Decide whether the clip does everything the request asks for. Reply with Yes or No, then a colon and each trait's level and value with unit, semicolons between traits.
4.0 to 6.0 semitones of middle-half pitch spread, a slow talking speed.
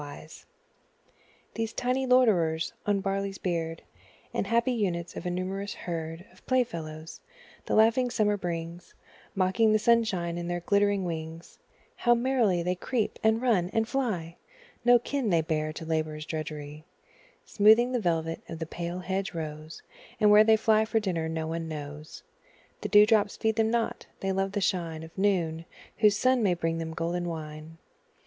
No: average, 5.1 semitones; average, 170 wpm